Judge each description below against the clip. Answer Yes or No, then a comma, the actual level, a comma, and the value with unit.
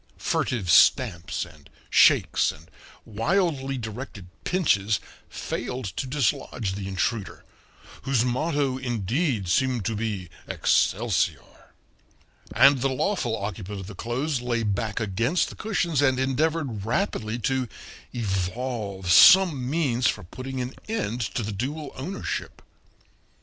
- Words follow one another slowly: Yes, slow, 120 wpm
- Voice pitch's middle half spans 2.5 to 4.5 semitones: No, average, 5.0 semitones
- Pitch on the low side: Yes, low, 120 Hz